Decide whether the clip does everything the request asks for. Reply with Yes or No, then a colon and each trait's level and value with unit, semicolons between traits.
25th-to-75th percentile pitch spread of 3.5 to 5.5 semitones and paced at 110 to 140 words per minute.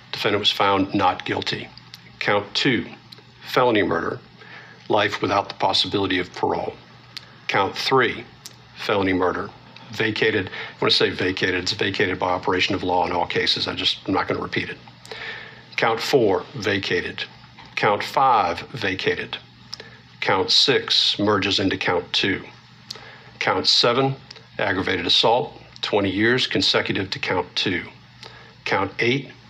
Yes: average, 4.4 semitones; slow, 135 wpm